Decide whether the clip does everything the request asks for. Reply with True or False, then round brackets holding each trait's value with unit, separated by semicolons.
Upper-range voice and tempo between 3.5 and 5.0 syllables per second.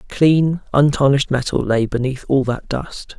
False (135 Hz; 4.5 syllables/s)